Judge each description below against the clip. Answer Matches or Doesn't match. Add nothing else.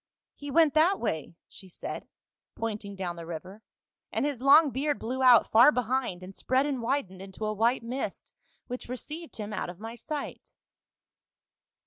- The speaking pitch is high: Matches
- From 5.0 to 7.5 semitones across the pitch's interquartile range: Matches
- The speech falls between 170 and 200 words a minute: Matches